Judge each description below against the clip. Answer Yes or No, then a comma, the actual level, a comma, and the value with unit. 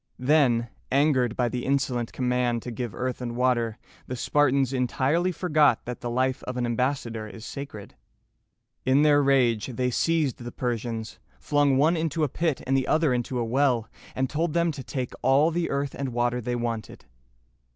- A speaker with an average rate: Yes, average, 180 wpm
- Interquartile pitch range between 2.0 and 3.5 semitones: Yes, average, 3.1 semitones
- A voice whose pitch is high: No, low, 130 Hz